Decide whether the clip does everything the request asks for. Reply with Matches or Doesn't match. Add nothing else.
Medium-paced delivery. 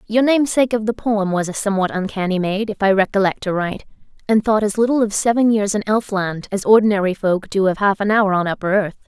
Doesn't match